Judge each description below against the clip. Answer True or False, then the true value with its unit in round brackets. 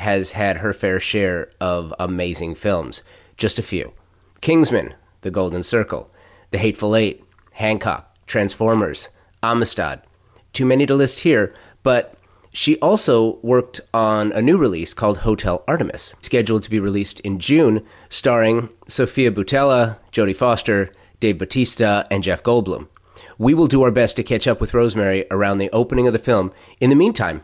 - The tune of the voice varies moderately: True (3.5 semitones)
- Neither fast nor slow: True (155 wpm)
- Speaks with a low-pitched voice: True (105 Hz)